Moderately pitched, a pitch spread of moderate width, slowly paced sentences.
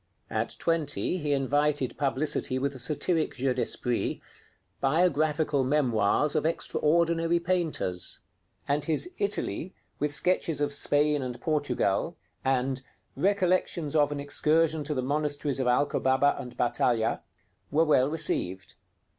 Yes: medium, 145 Hz; average, 3.1 semitones; slow, 120 wpm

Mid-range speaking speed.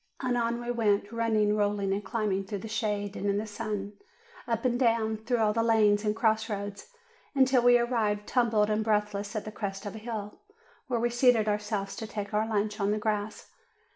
No: fast, 210 wpm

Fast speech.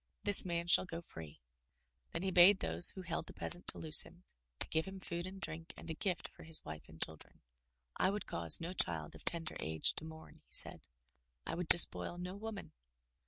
Yes: fast, 215 wpm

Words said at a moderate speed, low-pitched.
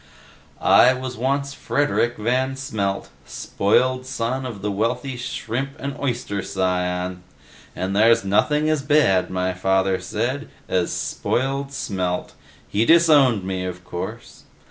No: slow, 125 wpm; low, 115 Hz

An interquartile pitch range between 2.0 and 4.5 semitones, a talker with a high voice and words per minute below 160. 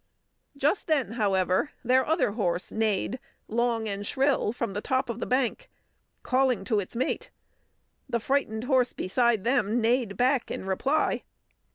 Yes: average, 4.0 semitones; high, 235 Hz; average, 150 wpm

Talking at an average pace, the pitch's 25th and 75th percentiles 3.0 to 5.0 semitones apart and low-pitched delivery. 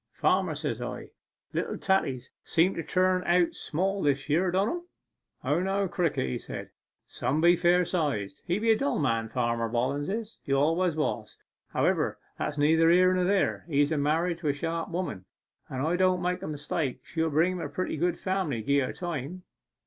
No: average, 190 wpm; average, 4.3 semitones; medium, 165 Hz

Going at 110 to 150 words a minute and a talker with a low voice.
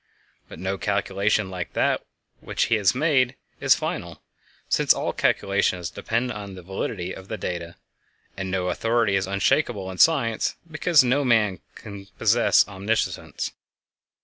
Yes: average, 140 wpm; low, 100 Hz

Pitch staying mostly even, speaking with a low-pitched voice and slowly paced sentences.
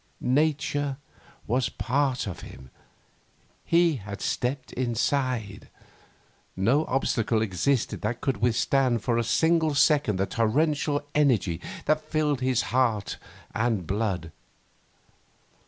No: average, 4.9 semitones; low, 125 Hz; slow, 105 wpm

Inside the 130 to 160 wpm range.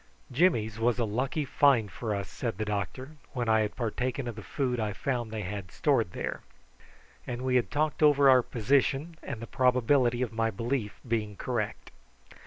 No: average, 185 wpm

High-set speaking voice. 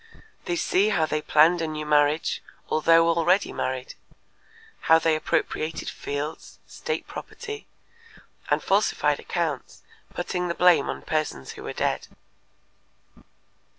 No: medium, 160 Hz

